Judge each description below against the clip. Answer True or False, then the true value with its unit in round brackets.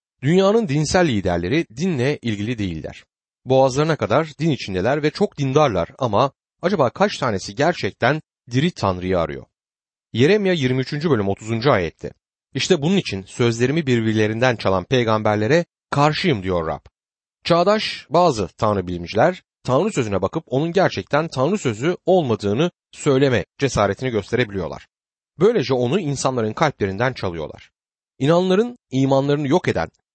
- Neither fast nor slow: True (120 wpm)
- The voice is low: True (130 Hz)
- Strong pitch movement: True (7.3 semitones)